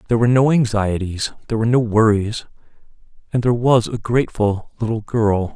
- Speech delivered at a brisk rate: No, average, 160 wpm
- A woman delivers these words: No, male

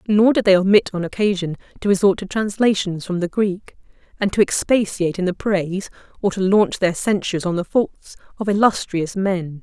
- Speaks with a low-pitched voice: No, high, 190 Hz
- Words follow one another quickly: No, average, 185 wpm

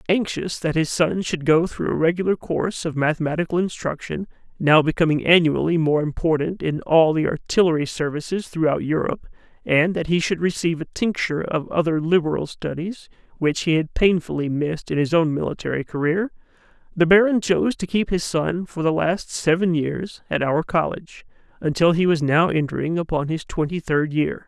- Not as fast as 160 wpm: No, average, 175 wpm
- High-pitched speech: No, medium, 165 Hz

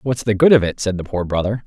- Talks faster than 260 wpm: Yes, fast, 325 wpm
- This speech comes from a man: Yes, male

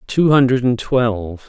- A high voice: No, low, 120 Hz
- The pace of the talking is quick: No, slow, 120 wpm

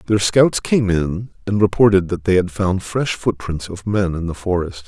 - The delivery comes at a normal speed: No, fast, 210 wpm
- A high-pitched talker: No, very low, 95 Hz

